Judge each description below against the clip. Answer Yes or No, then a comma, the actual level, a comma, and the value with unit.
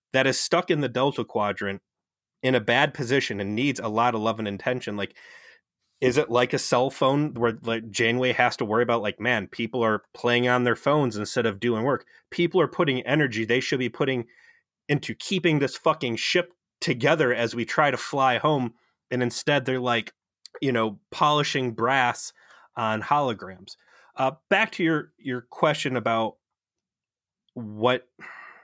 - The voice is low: Yes, low, 125 Hz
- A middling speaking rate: Yes, average, 175 wpm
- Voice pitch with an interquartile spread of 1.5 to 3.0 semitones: No, average, 3.8 semitones